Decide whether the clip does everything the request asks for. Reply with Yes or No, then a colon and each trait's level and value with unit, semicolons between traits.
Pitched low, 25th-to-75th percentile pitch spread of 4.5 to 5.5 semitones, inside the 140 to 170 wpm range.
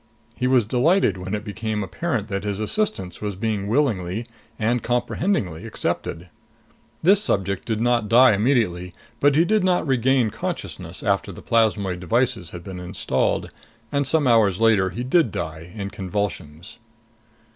Yes: low, 110 Hz; average, 5.0 semitones; average, 150 wpm